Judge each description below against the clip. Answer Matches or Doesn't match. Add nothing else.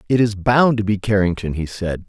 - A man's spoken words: Matches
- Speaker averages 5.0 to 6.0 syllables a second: Matches